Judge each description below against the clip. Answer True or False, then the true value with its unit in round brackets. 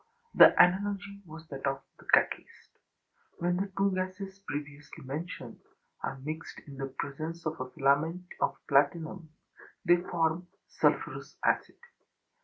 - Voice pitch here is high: False (160 Hz)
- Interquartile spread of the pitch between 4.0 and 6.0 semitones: True (4.6 semitones)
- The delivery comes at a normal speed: False (130 wpm)